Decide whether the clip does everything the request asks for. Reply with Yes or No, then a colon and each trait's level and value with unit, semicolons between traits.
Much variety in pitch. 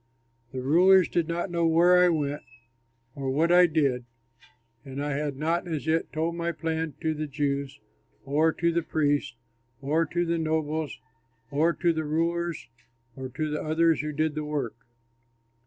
No: narrow, 2.5 semitones